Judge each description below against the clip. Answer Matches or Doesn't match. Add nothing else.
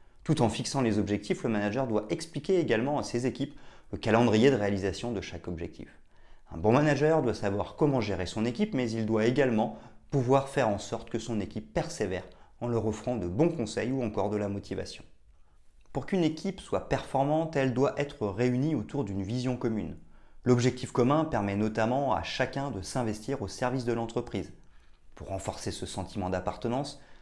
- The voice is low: Matches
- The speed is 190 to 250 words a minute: Doesn't match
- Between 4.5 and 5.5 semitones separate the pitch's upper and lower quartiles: Matches